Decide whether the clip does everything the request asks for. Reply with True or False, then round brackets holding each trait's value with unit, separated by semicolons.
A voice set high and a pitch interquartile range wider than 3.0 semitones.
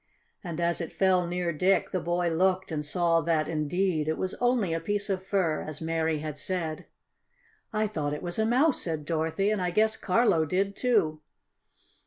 False (175 Hz; 3.4 semitones)